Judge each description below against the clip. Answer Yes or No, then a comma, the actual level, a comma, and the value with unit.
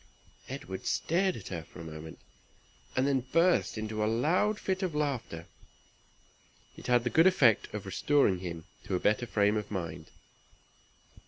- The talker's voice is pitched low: Yes, low, 115 Hz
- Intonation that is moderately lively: No, wide, 7.7 semitones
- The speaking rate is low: No, average, 160 wpm